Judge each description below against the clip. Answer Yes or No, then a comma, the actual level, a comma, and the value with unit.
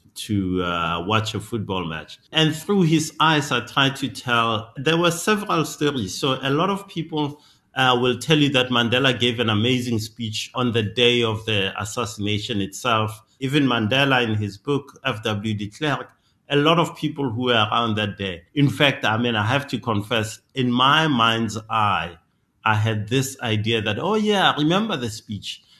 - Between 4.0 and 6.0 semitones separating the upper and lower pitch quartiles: Yes, average, 4.6 semitones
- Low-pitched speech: Yes, low, 120 Hz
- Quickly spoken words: No, average, 185 wpm